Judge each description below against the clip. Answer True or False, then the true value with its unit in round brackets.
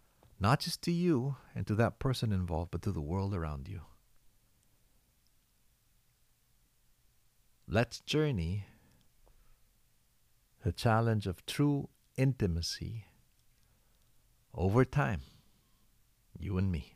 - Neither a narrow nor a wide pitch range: False (5.8 semitones)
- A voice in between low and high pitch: False (110 Hz)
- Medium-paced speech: False (95 wpm)